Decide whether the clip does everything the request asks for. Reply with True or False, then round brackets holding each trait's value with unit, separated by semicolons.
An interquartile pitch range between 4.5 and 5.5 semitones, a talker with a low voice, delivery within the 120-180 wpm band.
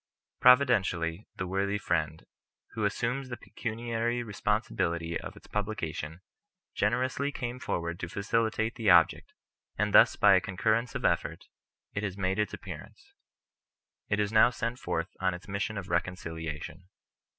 True (4.8 semitones; 100 Hz; 150 wpm)